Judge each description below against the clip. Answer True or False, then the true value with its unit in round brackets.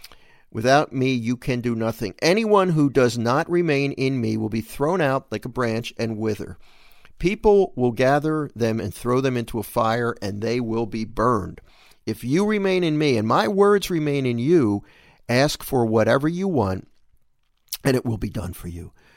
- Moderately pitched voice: False (125 Hz)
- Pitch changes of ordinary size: True (4.7 semitones)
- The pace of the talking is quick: False (190 wpm)